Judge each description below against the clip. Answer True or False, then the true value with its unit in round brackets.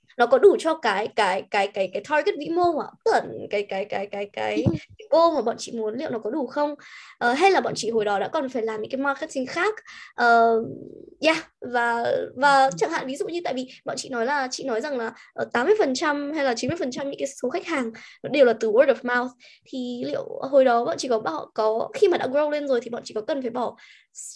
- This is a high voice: True (265 Hz)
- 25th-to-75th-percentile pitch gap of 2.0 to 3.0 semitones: False (5.5 semitones)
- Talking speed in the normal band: False (260 wpm)